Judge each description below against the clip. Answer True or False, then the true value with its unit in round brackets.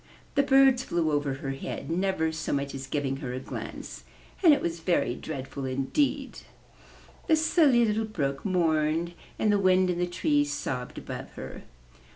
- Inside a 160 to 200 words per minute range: True (175 wpm)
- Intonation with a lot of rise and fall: True (6.6 semitones)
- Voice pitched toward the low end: False (165 Hz)